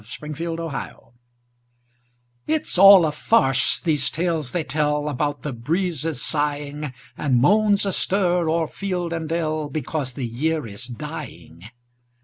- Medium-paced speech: No, slow, 125 wpm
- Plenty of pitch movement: No, average, 3.2 semitones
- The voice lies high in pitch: No, medium, 155 Hz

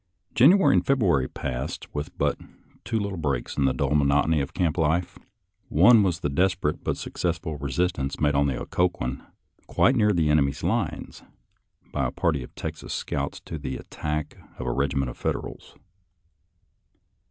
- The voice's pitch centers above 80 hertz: No, very low, 75 Hz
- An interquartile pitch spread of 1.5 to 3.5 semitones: No, average, 4.3 semitones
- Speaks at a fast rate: No, average, 160 wpm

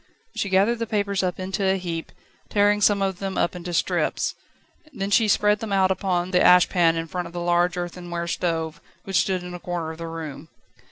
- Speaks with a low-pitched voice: No, medium, 180 Hz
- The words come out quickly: Yes, fast, 215 wpm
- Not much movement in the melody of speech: Yes, narrow, 2.2 semitones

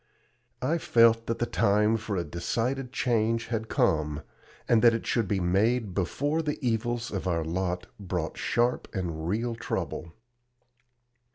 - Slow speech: No, average, 150 wpm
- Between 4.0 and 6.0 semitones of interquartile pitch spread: Yes, average, 4.8 semitones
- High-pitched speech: No, low, 110 Hz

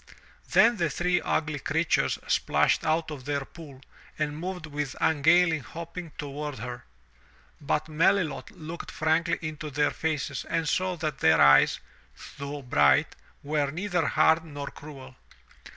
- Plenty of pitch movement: No, average, 2.7 semitones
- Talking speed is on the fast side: No, slow, 135 wpm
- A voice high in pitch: No, medium, 155 Hz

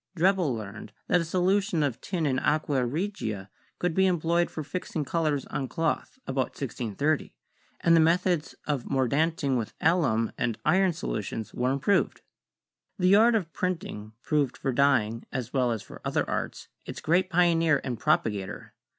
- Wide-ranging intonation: Yes, wide, 5.7 semitones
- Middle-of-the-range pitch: Yes, medium, 150 Hz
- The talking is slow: No, average, 160 wpm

